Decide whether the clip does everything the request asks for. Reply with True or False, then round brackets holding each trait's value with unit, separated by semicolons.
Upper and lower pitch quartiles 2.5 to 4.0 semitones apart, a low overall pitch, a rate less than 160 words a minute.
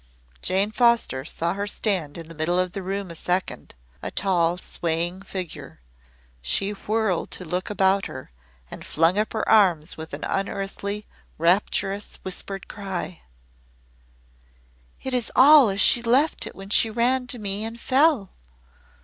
False (3.6 semitones; 195 Hz; 150 wpm)